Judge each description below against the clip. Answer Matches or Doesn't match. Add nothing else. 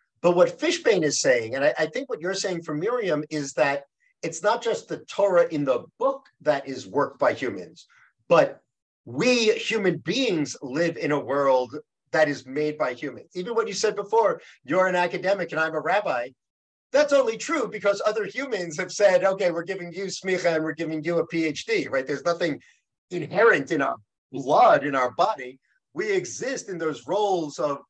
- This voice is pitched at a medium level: Matches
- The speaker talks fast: Doesn't match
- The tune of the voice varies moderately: Doesn't match